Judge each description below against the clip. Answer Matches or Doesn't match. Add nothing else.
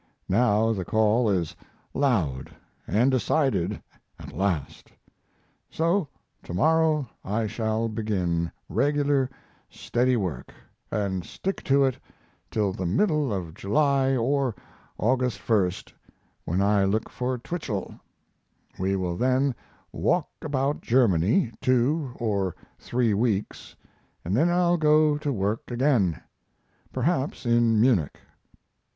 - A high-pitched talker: Doesn't match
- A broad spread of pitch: Matches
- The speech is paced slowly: Matches